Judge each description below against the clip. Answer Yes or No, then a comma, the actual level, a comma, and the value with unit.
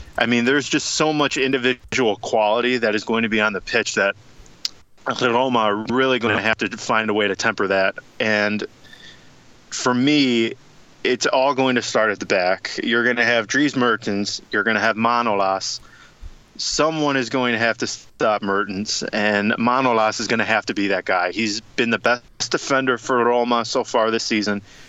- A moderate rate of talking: Yes, average, 190 wpm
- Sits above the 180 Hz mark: No, low, 115 Hz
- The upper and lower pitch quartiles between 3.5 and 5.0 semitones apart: No, average, 3.1 semitones